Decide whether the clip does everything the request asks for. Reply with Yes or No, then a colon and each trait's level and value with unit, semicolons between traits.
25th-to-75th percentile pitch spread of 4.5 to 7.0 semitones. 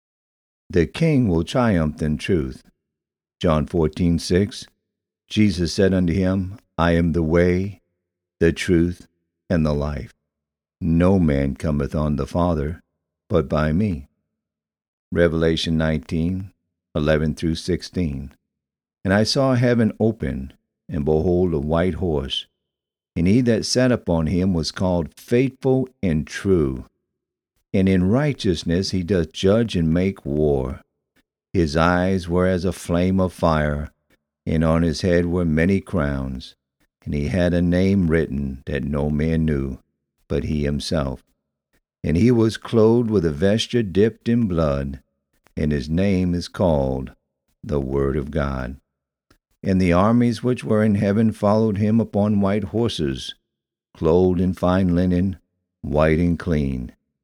No: average, 4.1 semitones